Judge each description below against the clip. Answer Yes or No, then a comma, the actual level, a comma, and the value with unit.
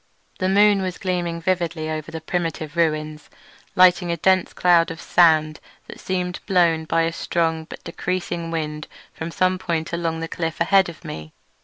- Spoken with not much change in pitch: Yes, narrow, 2.1 semitones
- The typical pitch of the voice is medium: Yes, medium, 170 Hz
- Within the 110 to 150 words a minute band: No, average, 170 wpm